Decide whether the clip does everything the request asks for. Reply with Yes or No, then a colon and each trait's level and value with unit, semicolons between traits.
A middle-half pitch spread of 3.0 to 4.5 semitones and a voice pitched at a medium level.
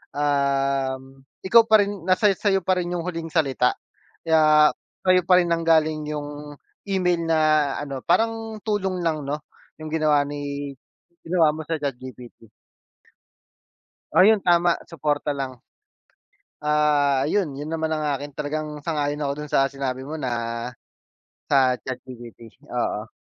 Yes: average, 3.6 semitones; medium, 150 Hz